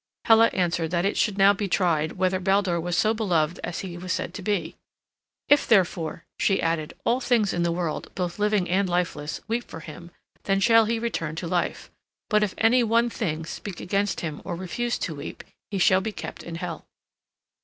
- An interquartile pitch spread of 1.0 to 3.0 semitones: No, average, 3.7 semitones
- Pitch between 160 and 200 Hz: Yes, medium, 185 Hz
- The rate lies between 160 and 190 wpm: No, average, 200 wpm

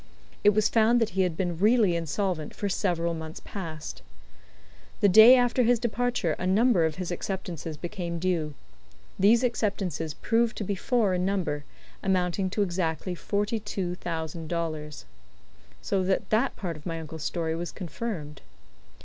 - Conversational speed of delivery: Yes, average, 160 wpm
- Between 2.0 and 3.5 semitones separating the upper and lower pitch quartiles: No, average, 4.2 semitones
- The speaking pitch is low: No, medium, 185 Hz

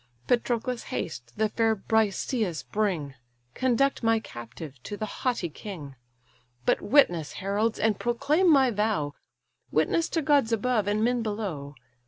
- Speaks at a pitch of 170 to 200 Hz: No, high, 215 Hz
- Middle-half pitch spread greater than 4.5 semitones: Yes, wide, 5.6 semitones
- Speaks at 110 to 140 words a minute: Yes, slow, 135 wpm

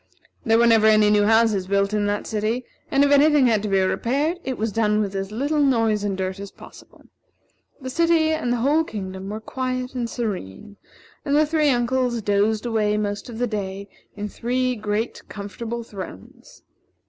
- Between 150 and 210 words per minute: Yes, average, 190 wpm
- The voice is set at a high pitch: Yes, high, 225 Hz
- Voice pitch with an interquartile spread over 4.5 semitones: No, average, 3.7 semitones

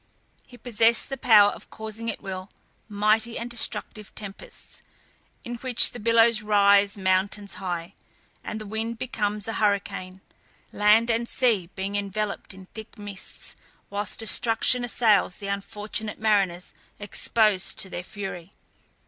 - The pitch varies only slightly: Yes, narrow, 2.2 semitones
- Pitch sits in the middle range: No, high, 210 Hz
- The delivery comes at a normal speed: No, slow, 130 wpm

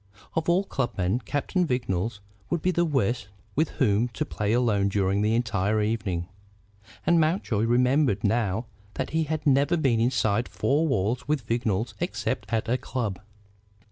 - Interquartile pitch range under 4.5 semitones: No, wide, 5.5 semitones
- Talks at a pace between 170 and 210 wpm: No, average, 160 wpm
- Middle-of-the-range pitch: No, low, 120 Hz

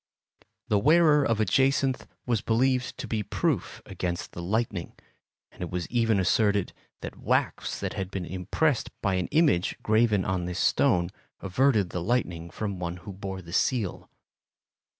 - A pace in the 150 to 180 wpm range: Yes, average, 160 wpm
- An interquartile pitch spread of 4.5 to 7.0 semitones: Yes, average, 5.1 semitones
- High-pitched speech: No, low, 100 Hz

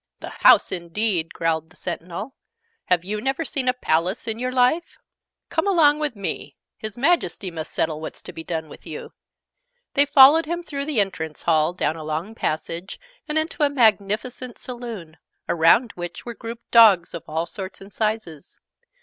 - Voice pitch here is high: Yes, high, 210 Hz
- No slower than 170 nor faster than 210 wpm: Yes, average, 175 wpm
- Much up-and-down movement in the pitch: Yes, wide, 7.2 semitones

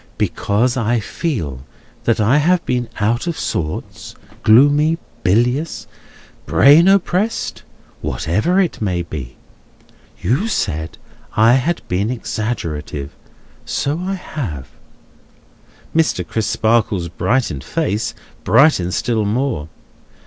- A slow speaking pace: Yes, slow, 100 wpm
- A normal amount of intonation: No, wide, 8.5 semitones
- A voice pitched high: No, low, 115 Hz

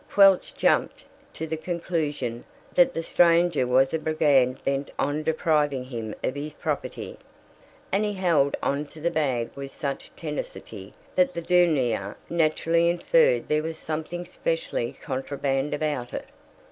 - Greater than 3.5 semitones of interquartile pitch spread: Yes, average, 4.1 semitones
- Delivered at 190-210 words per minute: No, average, 145 wpm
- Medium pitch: Yes, medium, 155 Hz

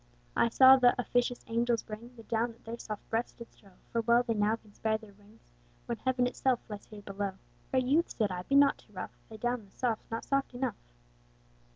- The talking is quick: Yes, fast, 215 wpm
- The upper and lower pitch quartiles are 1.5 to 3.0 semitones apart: Yes, narrow, 2.4 semitones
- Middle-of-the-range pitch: No, high, 230 Hz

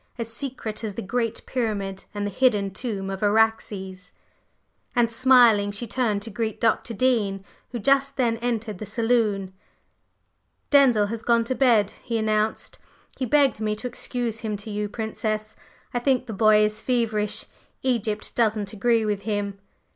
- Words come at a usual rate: Yes, average, 160 wpm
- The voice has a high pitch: Yes, high, 220 Hz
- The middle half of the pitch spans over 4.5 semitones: No, narrow, 2.6 semitones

